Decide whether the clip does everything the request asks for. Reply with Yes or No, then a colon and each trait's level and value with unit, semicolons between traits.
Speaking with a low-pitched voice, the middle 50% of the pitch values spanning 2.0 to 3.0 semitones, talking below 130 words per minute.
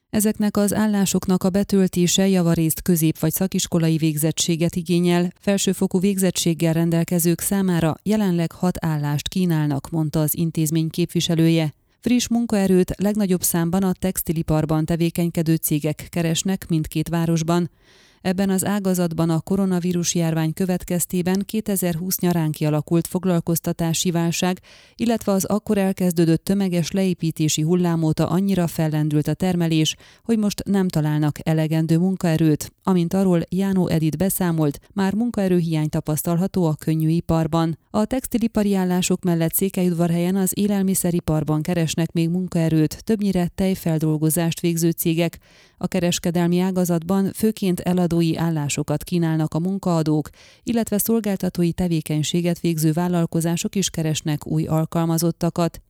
No: medium, 175 Hz; average, 2.7 semitones; average, 115 wpm